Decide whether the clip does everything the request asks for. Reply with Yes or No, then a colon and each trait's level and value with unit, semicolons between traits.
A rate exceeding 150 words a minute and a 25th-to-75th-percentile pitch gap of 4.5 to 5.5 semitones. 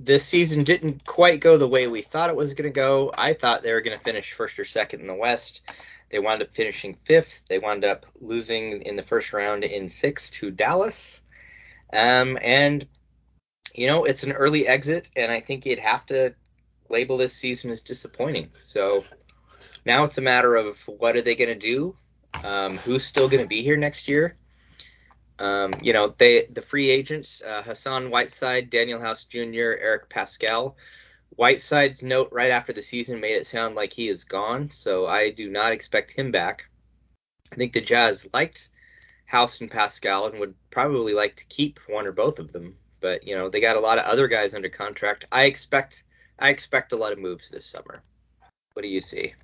Yes: average, 200 wpm; average, 5.2 semitones